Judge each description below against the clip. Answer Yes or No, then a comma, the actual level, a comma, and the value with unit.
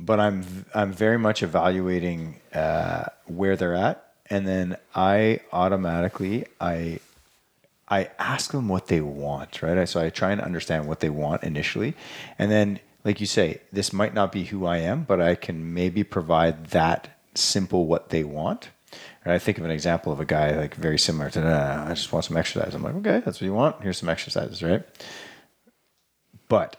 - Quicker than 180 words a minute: Yes, average, 190 wpm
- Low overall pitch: Yes, very low, 90 Hz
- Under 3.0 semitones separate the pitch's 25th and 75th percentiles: No, average, 3.3 semitones